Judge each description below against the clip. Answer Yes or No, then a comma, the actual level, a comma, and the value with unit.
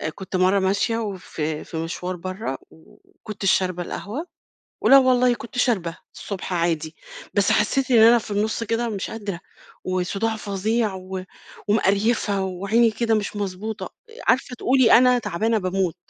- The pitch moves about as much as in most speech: Yes, average, 3.6 semitones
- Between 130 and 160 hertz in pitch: No, high, 205 Hz